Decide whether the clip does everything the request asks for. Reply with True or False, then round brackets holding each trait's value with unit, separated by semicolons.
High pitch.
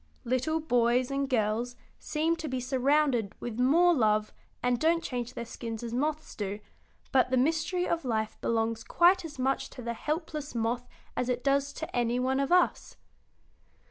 True (255 Hz)